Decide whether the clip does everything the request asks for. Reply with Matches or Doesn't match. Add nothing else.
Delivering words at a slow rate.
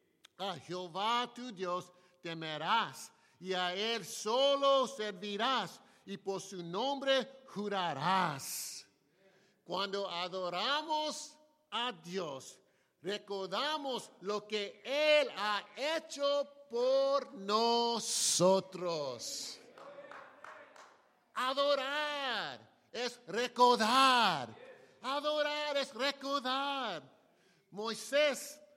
Matches